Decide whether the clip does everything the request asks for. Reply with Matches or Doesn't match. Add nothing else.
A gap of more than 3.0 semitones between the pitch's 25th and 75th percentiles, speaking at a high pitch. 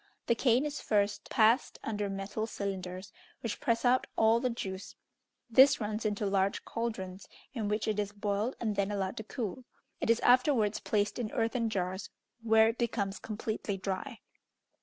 Doesn't match